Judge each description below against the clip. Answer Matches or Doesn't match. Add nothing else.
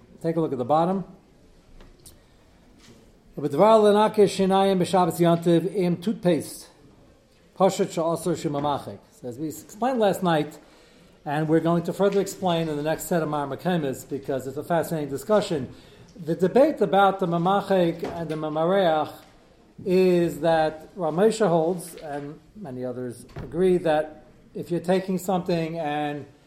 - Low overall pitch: Doesn't match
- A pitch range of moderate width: Matches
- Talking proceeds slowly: Matches